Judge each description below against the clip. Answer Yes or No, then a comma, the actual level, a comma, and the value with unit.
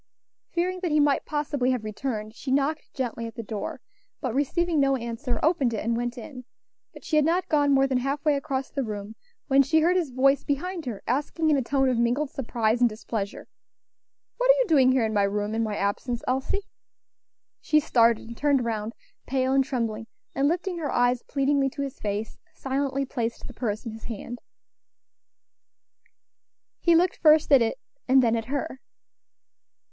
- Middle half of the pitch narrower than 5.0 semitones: Yes, average, 4.0 semitones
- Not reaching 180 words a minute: No, average, 190 wpm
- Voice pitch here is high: Yes, very high, 265 Hz